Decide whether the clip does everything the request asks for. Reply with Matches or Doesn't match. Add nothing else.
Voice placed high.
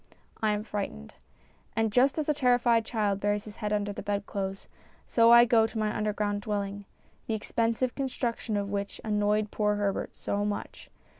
Matches